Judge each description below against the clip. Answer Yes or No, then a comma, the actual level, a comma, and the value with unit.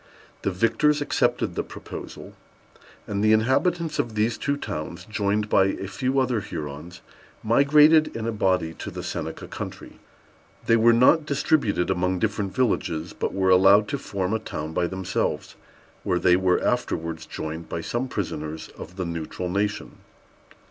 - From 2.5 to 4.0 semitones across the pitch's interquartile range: No, average, 4.9 semitones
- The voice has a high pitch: No, low, 100 Hz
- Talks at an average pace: Yes, average, 155 wpm